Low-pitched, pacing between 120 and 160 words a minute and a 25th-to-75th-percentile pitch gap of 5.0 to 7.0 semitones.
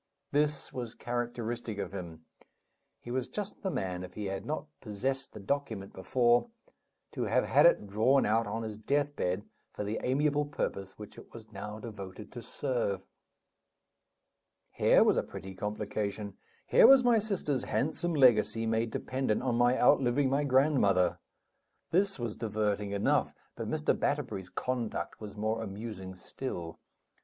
No: low, 115 Hz; average, 150 wpm; average, 4.6 semitones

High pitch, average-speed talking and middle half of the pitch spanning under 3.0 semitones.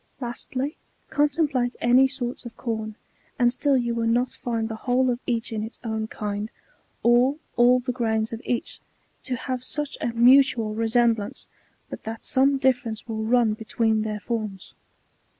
Yes: high, 240 Hz; average, 165 wpm; narrow, 2.4 semitones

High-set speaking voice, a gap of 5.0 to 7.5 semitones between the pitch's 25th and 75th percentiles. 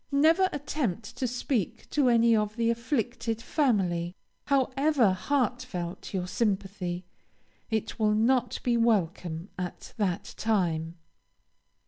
Yes: high, 225 Hz; average, 5.3 semitones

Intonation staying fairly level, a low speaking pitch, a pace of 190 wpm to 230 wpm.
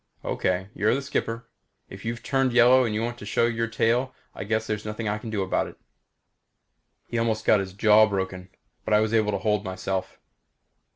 Yes: narrow, 2.3 semitones; low, 110 Hz; average, 195 wpm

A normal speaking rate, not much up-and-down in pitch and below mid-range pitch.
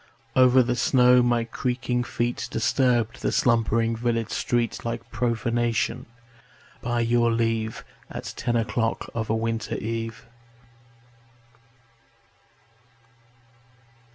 No: slow, 100 wpm; narrow, 1.2 semitones; low, 115 Hz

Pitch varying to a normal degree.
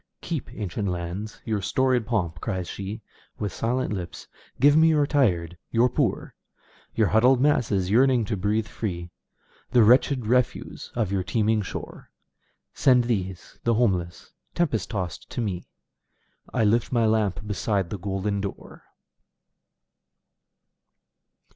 Yes: average, 4.2 semitones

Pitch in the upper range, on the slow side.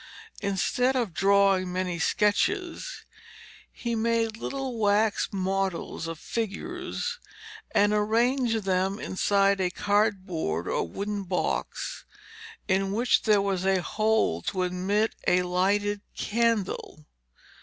Yes: high, 200 Hz; slow, 110 wpm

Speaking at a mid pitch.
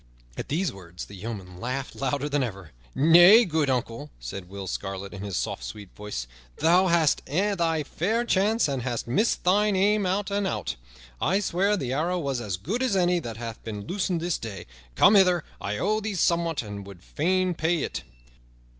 Yes: medium, 155 Hz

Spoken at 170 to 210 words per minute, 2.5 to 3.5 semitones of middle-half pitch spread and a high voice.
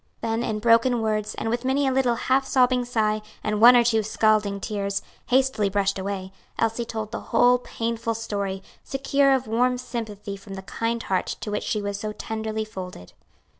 Yes: average, 185 wpm; average, 2.9 semitones; high, 225 Hz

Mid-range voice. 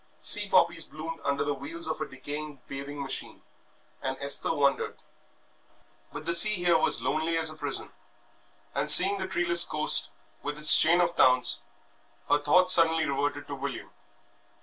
Yes: medium, 155 Hz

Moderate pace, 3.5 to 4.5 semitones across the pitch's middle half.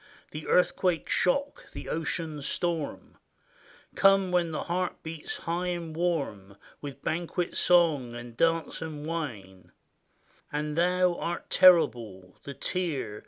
No: slow, 125 wpm; average, 3.9 semitones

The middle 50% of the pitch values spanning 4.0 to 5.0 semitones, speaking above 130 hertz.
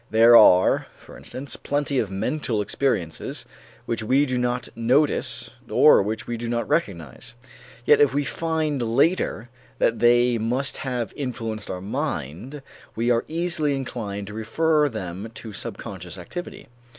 No: average, 4.6 semitones; low, 120 Hz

